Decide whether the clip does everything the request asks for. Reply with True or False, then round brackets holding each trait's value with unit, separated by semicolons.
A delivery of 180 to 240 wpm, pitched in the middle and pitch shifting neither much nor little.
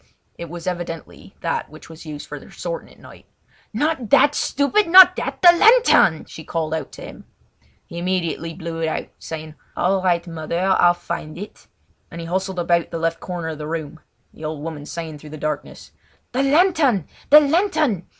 False (185 wpm; 170 Hz; 7.9 semitones)